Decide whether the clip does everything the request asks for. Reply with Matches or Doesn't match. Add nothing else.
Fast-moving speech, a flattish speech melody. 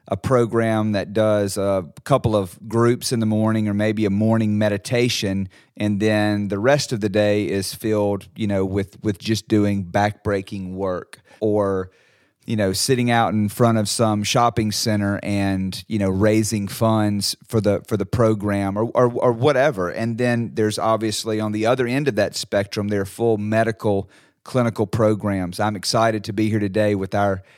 Doesn't match